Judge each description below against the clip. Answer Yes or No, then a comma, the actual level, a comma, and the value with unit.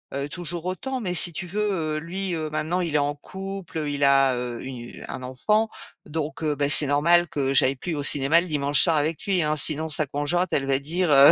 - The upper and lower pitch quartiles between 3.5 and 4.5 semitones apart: Yes, average, 3.8 semitones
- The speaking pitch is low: No, medium, 155 Hz